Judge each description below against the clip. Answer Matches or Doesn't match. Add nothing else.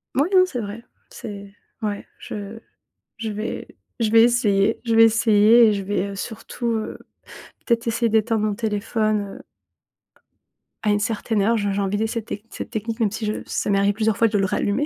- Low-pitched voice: Doesn't match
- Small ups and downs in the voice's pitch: Matches